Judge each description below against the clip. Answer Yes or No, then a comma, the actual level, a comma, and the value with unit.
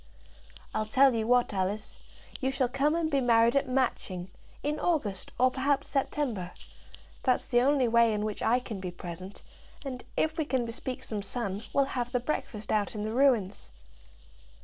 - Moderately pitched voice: No, high, 245 Hz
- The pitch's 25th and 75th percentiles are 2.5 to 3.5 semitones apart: No, average, 4.3 semitones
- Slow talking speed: No, average, 175 wpm